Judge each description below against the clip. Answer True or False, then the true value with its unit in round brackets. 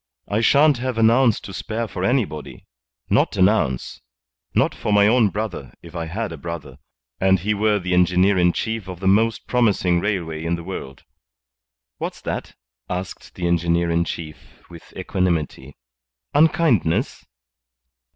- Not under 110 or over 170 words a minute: True (155 wpm)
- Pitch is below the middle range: True (95 Hz)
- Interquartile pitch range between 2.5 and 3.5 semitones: False (4.4 semitones)